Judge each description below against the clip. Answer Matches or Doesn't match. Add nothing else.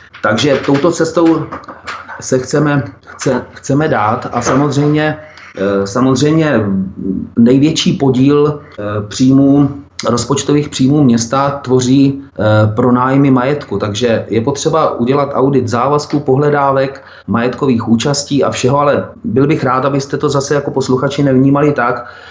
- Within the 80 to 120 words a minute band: Matches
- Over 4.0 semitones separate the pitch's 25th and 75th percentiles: Doesn't match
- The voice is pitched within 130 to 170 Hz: Matches